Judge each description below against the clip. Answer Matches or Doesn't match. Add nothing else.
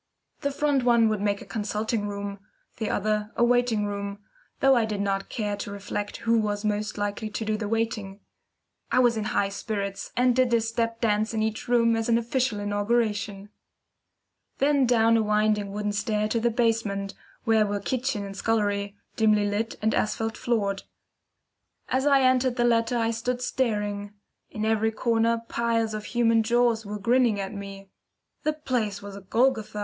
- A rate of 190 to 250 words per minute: Doesn't match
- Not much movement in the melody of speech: Matches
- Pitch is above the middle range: Matches